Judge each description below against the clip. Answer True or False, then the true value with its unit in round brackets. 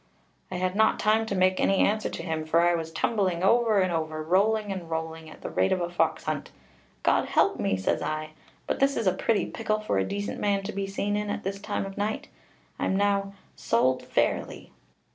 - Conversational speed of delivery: False (225 wpm)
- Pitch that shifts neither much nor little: True (4.1 semitones)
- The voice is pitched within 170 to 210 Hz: True (190 Hz)